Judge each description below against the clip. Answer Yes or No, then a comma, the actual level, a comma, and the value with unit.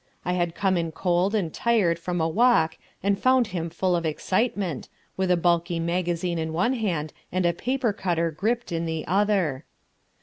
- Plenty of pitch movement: No, average, 3.2 semitones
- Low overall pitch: No, medium, 175 Hz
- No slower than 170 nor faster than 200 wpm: Yes, average, 180 wpm